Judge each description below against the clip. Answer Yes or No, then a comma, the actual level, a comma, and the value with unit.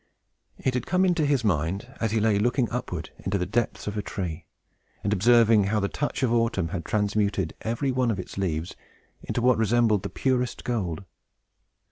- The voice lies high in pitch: No, low, 110 Hz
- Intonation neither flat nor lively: Yes, average, 3.9 semitones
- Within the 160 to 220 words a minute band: Yes, average, 190 wpm